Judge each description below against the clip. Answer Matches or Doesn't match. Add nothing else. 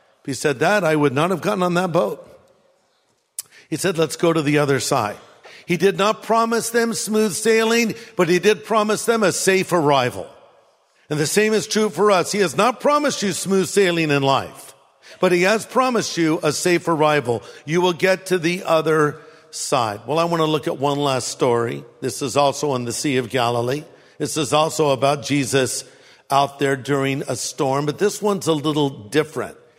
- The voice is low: Doesn't match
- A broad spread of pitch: Matches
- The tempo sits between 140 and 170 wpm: Doesn't match